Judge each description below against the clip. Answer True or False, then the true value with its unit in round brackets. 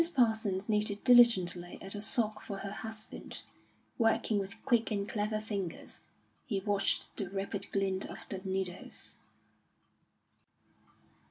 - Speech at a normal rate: False (120 wpm)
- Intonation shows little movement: True (2.2 semitones)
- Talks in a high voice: True (205 Hz)